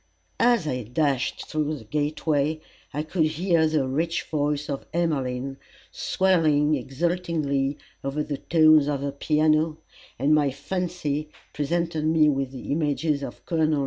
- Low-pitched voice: No, medium, 150 Hz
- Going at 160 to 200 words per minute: No, average, 140 wpm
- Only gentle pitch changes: Yes, narrow, 2.3 semitones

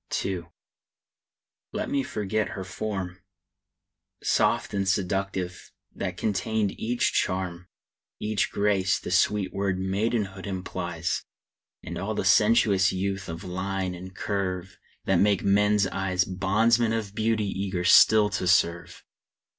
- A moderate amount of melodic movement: No, narrow, 2.0 semitones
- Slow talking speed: Yes, slow, 125 wpm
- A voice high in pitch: No, very low, 95 Hz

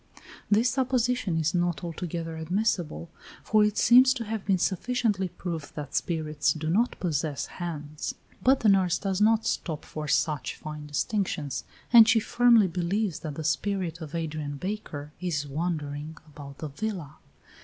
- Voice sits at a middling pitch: Yes, medium, 170 Hz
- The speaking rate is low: No, average, 155 wpm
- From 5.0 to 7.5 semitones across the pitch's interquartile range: Yes, wide, 5.5 semitones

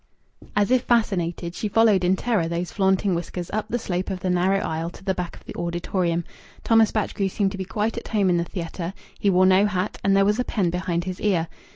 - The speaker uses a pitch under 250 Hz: Yes, high, 190 Hz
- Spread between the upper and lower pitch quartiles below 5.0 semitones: Yes, average, 2.8 semitones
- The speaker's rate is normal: No, fast, 235 wpm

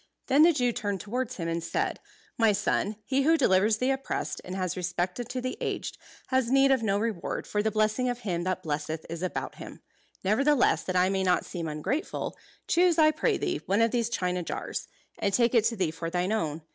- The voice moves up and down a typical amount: No, wide, 5.8 semitones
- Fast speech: Yes, fast, 215 wpm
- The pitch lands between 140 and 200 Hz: No, high, 215 Hz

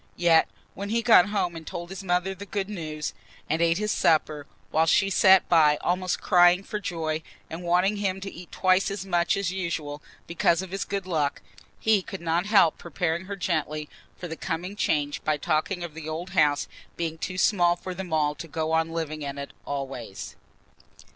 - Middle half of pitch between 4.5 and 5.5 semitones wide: No, average, 3.3 semitones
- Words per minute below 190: No, average, 195 wpm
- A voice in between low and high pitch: Yes, medium, 175 Hz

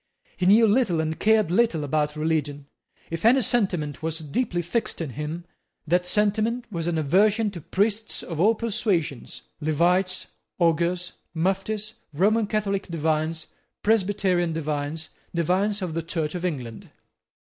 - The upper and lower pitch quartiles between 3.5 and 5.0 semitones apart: Yes, average, 4.7 semitones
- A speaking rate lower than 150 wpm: Yes, slow, 135 wpm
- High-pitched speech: No, medium, 175 Hz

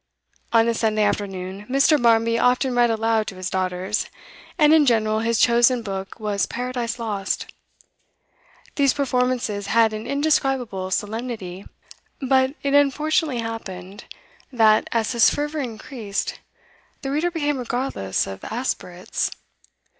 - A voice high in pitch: Yes, high, 230 Hz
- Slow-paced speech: Yes, slow, 125 wpm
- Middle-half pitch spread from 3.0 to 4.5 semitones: Yes, average, 4.0 semitones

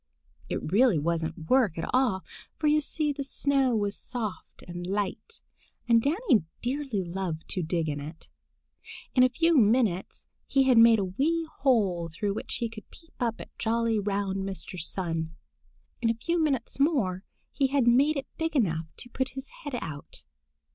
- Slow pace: No, average, 175 wpm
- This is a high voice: Yes, high, 230 Hz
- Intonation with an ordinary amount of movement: No, wide, 6.6 semitones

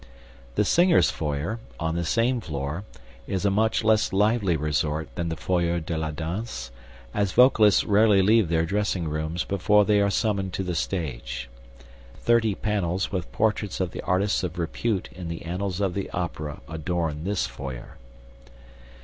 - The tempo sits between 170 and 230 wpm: No, average, 160 wpm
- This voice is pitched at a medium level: No, very low, 90 Hz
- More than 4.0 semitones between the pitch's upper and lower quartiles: Yes, average, 4.4 semitones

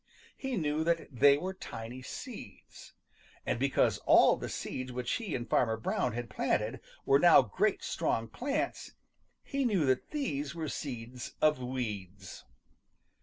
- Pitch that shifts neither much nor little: No, wide, 5.7 semitones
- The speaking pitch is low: Yes, low, 130 Hz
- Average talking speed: Yes, average, 145 wpm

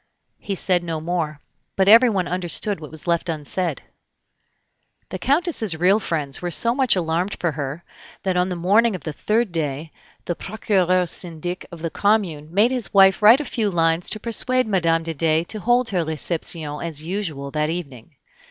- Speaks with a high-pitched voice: No, medium, 175 Hz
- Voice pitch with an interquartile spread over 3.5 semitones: Yes, average, 4.2 semitones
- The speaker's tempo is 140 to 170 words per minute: No, average, 180 wpm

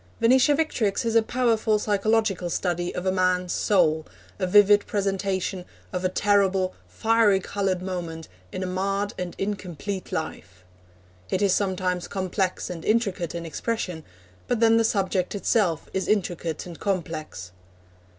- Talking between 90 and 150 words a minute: Yes, average, 140 wpm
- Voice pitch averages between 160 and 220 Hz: Yes, high, 190 Hz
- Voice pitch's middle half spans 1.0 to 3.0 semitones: Yes, narrow, 2.6 semitones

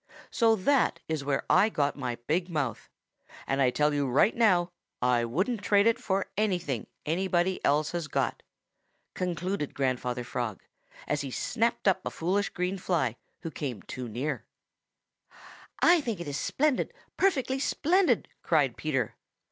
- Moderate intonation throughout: No, wide, 6.9 semitones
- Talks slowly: No, average, 150 wpm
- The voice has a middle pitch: Yes, medium, 170 Hz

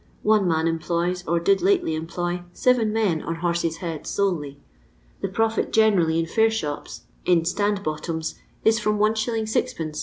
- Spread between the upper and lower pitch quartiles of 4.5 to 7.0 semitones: Yes, average, 4.8 semitones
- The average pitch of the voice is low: No, medium, 175 Hz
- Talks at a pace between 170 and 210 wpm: No, average, 155 wpm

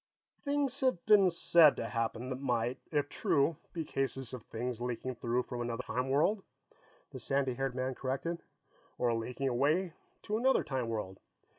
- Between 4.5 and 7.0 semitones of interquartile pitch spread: Yes, average, 5.1 semitones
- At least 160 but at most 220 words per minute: Yes, average, 170 wpm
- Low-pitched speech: Yes, low, 130 Hz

